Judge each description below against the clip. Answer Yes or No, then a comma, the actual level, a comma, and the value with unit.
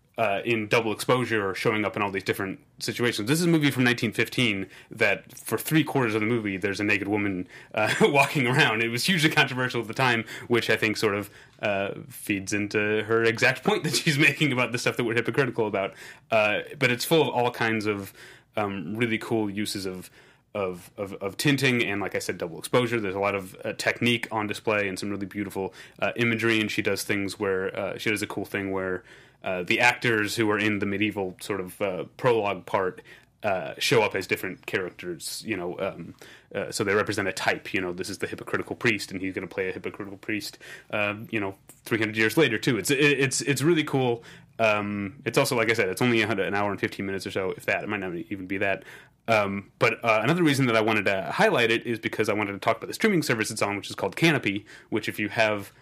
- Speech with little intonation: No, average, 3.6 semitones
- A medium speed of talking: No, fast, 235 wpm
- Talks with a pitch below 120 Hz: Yes, low, 110 Hz